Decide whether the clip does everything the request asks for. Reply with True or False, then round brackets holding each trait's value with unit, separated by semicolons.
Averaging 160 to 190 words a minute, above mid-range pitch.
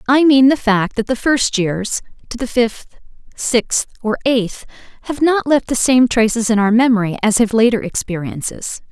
True (180 wpm; 235 Hz)